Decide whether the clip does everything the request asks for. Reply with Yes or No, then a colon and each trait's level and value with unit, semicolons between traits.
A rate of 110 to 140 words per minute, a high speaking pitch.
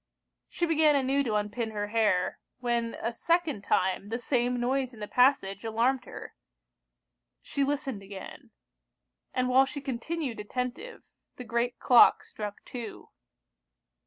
Yes: slow, 135 wpm; high, 245 Hz